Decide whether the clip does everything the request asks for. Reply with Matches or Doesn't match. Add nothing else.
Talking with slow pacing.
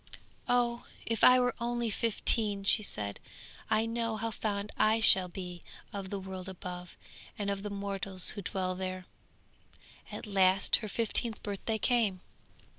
Doesn't match